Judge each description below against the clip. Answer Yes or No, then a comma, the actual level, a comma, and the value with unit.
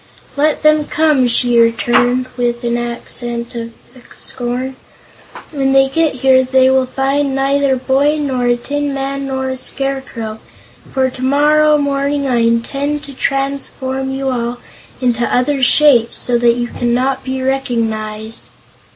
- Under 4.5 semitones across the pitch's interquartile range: Yes, narrow, 2.4 semitones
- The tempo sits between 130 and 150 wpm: Yes, average, 140 wpm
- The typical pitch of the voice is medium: No, very high, 265 Hz